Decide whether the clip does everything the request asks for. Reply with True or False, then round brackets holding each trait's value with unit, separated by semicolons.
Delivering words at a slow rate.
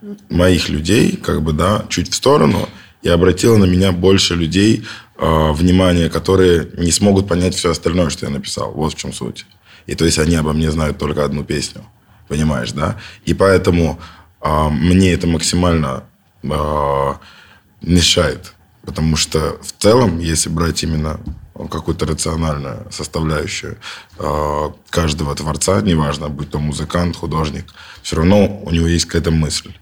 False (150 wpm)